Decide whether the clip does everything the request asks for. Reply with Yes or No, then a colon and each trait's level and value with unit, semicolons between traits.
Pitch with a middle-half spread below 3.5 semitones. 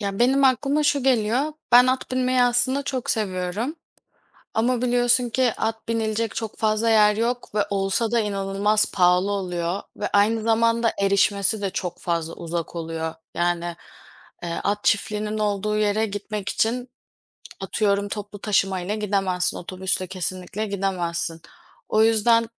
Yes: average, 3.1 semitones